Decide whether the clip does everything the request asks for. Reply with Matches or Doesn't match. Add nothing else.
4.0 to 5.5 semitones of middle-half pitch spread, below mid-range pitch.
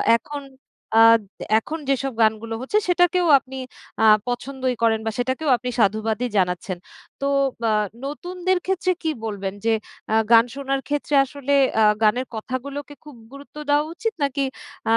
Doesn't match